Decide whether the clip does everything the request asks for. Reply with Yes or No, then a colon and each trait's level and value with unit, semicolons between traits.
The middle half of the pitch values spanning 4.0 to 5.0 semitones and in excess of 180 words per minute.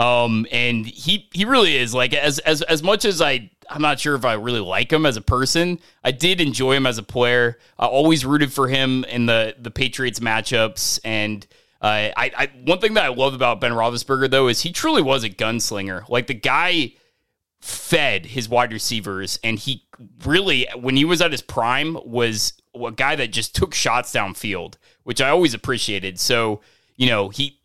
Yes: average, 4.6 semitones; average, 200 wpm